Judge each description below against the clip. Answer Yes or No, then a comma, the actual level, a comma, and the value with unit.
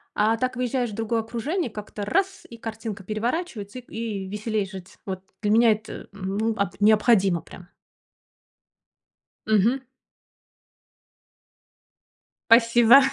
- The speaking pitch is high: Yes, high, 220 Hz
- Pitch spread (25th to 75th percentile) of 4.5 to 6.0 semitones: No, average, 2.8 semitones